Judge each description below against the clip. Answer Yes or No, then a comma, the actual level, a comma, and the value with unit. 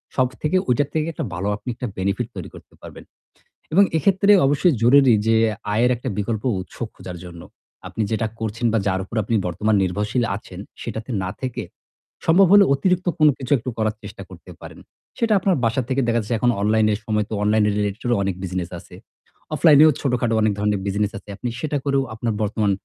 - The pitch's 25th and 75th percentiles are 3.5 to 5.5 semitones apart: Yes, average, 4.7 semitones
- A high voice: No, low, 115 Hz